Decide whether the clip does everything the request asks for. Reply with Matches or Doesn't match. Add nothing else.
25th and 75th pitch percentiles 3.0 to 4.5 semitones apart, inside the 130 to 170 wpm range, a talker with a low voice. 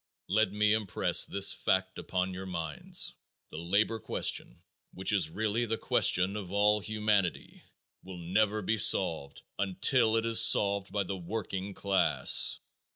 Doesn't match